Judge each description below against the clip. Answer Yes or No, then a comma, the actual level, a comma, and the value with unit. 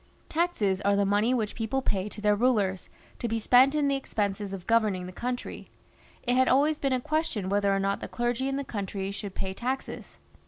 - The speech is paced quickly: Yes, fast, 210 wpm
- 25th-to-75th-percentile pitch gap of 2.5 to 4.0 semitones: No, average, 4.6 semitones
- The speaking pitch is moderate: No, high, 220 Hz